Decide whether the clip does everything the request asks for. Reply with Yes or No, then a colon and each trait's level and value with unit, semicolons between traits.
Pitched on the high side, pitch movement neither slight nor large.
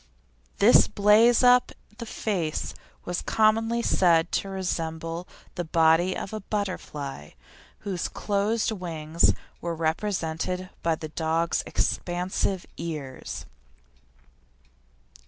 No: medium, 180 Hz; average, 4.1 semitones